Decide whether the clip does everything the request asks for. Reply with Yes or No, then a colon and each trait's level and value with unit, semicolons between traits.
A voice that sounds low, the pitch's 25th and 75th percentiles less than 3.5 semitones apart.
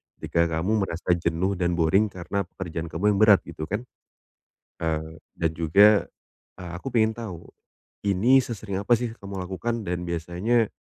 No: very low, 95 Hz; average, 4.0 semitones